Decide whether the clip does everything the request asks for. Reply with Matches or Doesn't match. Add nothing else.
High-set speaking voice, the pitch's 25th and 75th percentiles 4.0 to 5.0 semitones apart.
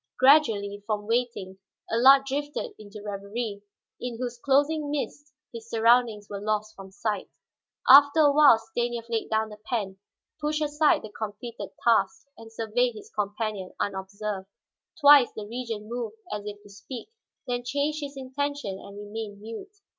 Matches